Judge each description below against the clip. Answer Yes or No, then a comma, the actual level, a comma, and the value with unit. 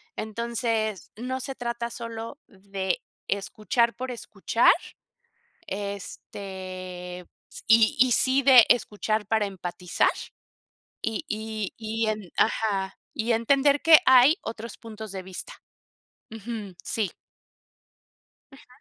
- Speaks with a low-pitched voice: No, high, 220 Hz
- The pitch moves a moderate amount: Yes, average, 3.1 semitones